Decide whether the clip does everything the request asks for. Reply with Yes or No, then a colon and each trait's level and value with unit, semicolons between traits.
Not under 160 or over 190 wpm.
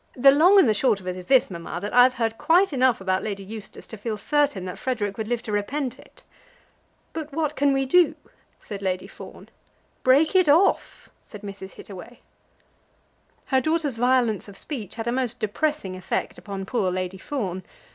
Yes: average, 185 wpm